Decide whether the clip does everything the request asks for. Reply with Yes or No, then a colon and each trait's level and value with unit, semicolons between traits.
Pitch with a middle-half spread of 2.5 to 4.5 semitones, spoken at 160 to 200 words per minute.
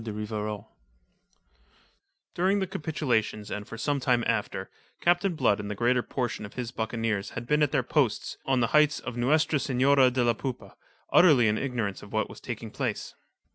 No: average, 4.9 semitones; average, 180 wpm